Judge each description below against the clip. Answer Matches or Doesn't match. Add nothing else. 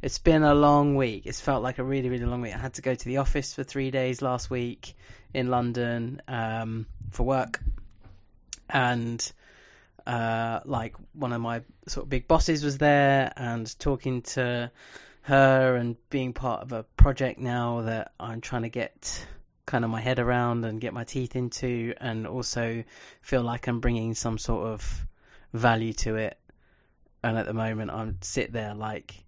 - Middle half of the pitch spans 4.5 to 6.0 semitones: Doesn't match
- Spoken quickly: Doesn't match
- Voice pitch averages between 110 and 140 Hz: Matches